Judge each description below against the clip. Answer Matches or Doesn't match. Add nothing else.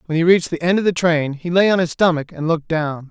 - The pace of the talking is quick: Matches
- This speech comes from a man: Matches